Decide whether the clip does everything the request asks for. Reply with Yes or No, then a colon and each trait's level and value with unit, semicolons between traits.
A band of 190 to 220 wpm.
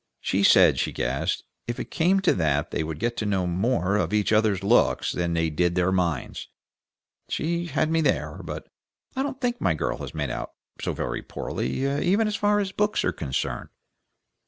Yes: average, 200 wpm